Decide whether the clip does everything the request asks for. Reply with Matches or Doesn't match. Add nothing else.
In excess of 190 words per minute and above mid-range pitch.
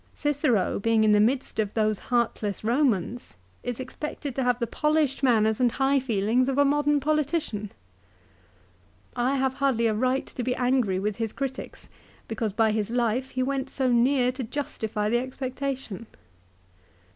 Doesn't match